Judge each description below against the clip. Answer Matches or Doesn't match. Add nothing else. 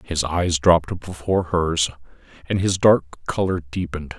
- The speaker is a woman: Doesn't match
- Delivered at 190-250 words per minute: Doesn't match